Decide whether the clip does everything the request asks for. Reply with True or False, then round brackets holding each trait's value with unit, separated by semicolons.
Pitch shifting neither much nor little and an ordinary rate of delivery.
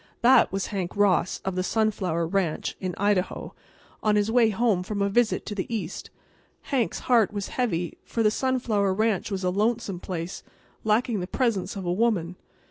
True (3.5 semitones; 180 wpm)